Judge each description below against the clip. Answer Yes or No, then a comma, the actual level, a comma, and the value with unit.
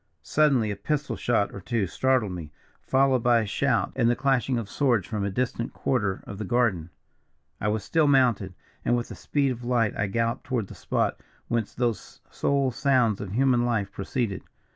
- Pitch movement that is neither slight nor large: Yes, average, 4.1 semitones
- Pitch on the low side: Yes, low, 120 Hz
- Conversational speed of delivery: Yes, average, 190 wpm